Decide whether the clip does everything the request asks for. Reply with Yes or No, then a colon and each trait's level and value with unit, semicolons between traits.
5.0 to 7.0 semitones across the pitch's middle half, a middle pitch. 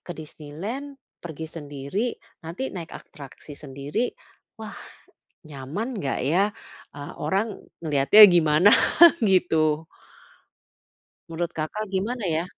Yes: average, 5.3 semitones; medium, 165 Hz